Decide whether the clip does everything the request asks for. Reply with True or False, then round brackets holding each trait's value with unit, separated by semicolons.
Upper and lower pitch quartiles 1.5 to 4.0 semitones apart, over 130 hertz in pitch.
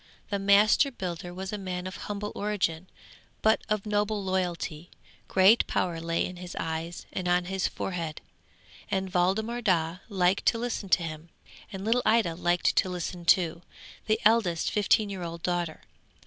True (3.0 semitones; 185 Hz)